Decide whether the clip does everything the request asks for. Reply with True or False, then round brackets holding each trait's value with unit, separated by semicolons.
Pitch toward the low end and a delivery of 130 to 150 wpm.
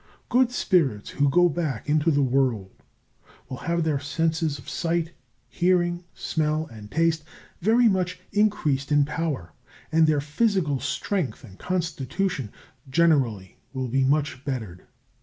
False (155 Hz; 135 wpm)